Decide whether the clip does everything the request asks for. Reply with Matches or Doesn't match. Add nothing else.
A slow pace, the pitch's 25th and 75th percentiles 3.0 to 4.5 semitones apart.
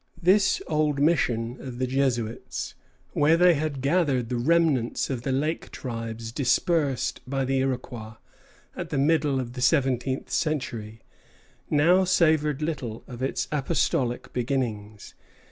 Matches